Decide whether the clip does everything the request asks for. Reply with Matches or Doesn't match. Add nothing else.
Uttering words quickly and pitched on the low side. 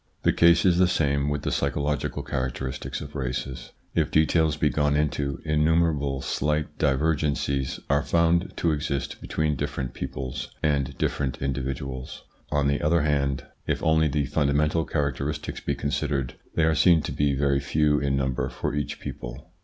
Doesn't match